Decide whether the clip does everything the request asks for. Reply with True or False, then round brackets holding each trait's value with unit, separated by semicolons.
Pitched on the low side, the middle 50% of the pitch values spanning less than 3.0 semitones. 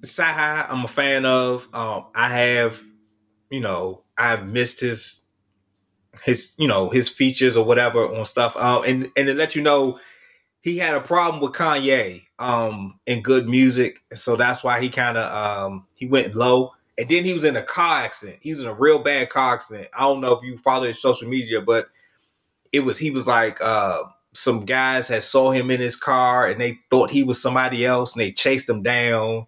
True (125 Hz; 2.5 semitones)